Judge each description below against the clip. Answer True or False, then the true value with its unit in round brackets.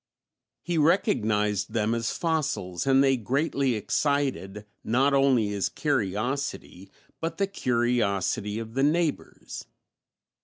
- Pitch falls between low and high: False (125 Hz)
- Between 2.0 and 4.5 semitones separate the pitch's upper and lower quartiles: False (5.3 semitones)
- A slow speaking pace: True (110 wpm)